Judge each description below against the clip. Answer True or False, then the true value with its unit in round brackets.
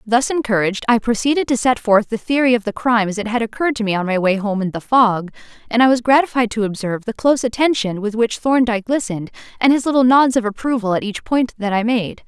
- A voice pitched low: False (230 Hz)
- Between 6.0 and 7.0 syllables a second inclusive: True (6.4 syllables/s)